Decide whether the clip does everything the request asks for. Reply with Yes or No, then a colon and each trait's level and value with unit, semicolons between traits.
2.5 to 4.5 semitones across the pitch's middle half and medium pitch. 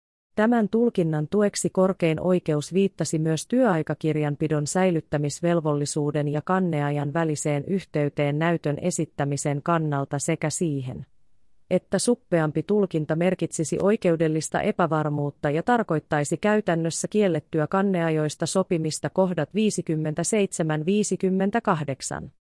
Yes: average, 3.7 semitones; medium, 165 Hz